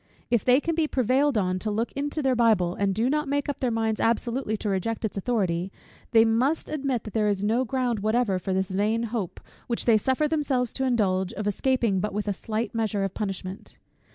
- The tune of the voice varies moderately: Yes, average, 4.1 semitones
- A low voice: No, high, 225 Hz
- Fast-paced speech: Yes, fast, 215 wpm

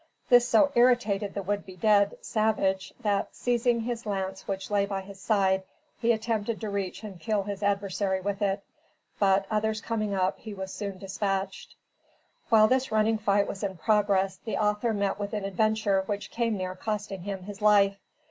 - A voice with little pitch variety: Yes, narrow, 2.0 semitones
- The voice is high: Yes, high, 205 Hz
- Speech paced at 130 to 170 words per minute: No, average, 180 wpm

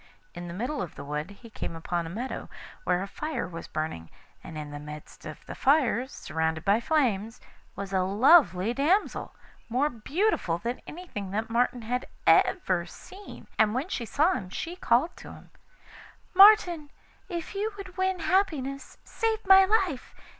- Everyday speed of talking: Yes, average, 170 wpm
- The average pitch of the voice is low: No, high, 245 Hz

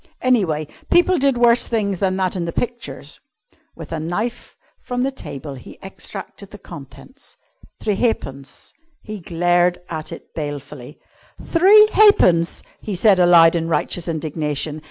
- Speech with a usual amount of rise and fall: No, wide, 6.7 semitones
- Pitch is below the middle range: No, medium, 180 Hz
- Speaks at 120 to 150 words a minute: Yes, average, 140 wpm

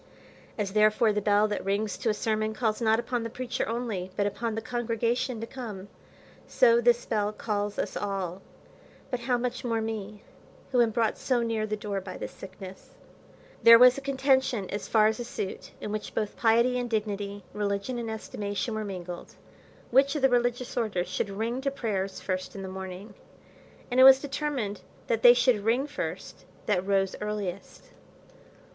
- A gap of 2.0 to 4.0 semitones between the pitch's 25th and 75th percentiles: Yes, average, 3.0 semitones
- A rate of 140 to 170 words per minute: No, average, 180 wpm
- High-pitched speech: Yes, high, 220 Hz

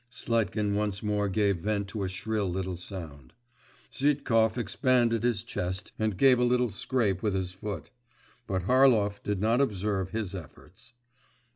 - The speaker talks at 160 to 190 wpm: No, average, 150 wpm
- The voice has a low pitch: Yes, low, 105 Hz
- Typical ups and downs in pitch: Yes, average, 3.4 semitones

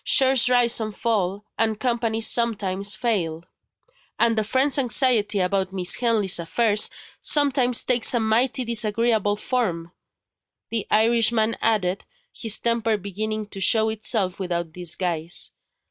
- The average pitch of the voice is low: No, high, 220 Hz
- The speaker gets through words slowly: Yes, slow, 130 wpm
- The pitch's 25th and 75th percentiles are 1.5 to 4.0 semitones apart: Yes, average, 3.2 semitones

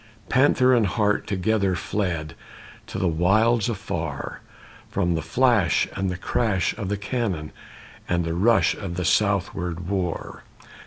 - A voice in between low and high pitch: No, very low, 95 Hz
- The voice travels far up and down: No, average, 3.8 semitones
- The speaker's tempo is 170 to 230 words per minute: No, average, 140 wpm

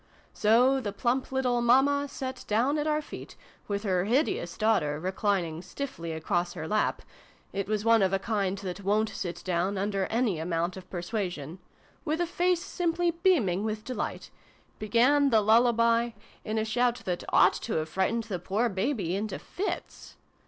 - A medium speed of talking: Yes, average, 170 wpm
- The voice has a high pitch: Yes, high, 215 Hz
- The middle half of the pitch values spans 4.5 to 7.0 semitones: Yes, average, 5.1 semitones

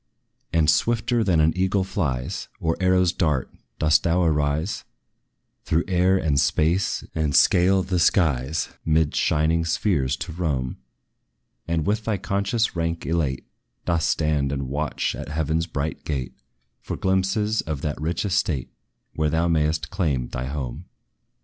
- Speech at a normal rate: Yes, average, 145 wpm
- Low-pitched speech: Yes, very low, 80 Hz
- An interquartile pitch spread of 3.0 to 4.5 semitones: Yes, average, 3.6 semitones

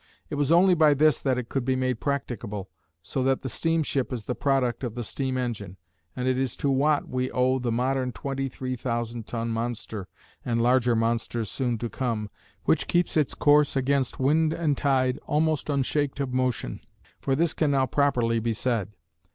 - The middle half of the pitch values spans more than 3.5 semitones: No, average, 3.0 semitones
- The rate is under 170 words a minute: No, average, 190 wpm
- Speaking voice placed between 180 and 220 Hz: No, low, 130 Hz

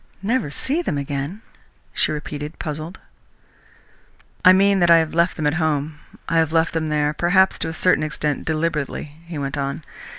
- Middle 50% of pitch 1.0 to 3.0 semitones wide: Yes, average, 2.7 semitones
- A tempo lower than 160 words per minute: No, average, 175 wpm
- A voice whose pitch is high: No, medium, 160 Hz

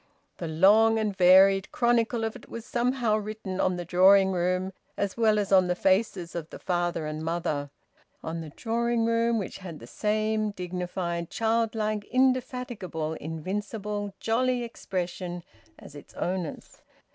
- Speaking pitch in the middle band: No, high, 195 Hz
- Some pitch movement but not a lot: Yes, average, 4.2 semitones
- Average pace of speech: Yes, average, 145 wpm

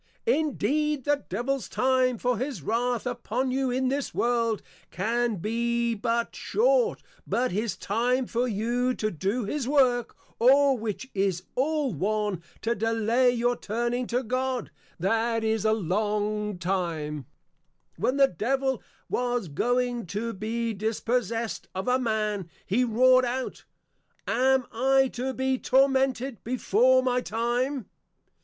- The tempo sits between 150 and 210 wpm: No, slow, 135 wpm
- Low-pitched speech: No, high, 240 Hz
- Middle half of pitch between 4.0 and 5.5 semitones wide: No, average, 3.0 semitones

